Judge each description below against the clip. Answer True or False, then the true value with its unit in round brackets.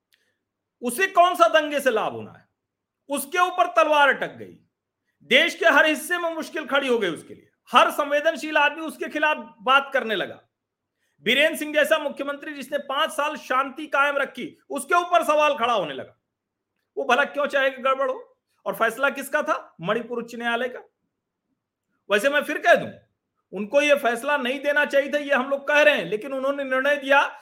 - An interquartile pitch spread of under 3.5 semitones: True (2.4 semitones)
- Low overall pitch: False (290 Hz)